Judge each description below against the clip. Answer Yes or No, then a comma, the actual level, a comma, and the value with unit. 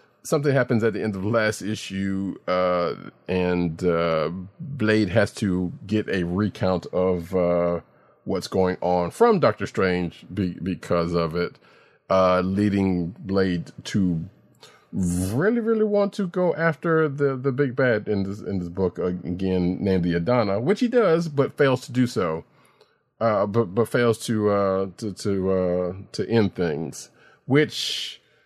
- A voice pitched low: Yes, very low, 95 Hz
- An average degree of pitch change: Yes, average, 5.0 semitones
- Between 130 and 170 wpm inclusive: Yes, average, 160 wpm